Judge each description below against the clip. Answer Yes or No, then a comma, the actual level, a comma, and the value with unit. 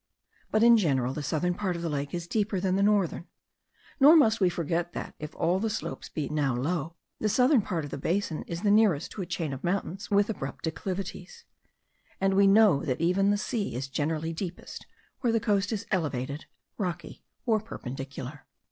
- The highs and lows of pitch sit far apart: No, average, 5.0 semitones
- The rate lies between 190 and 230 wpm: Yes, average, 195 wpm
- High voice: No, medium, 180 Hz